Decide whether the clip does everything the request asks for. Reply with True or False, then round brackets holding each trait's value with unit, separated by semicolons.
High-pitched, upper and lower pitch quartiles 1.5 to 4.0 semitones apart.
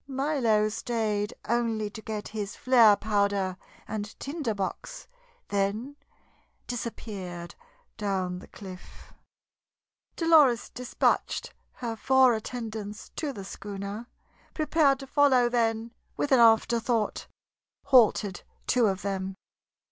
True (225 Hz; 3.6 semitones)